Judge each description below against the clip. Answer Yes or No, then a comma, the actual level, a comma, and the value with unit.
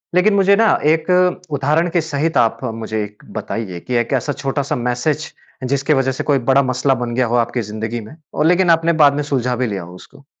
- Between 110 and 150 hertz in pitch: Yes, medium, 140 Hz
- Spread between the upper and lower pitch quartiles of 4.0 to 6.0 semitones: Yes, average, 5.0 semitones